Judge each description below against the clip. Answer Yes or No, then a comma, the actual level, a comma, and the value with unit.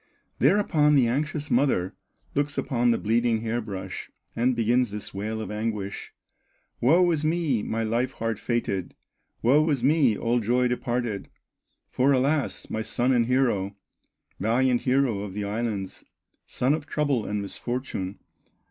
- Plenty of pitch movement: No, average, 3.8 semitones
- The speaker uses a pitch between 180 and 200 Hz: No, low, 120 Hz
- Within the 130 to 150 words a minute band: Yes, average, 145 wpm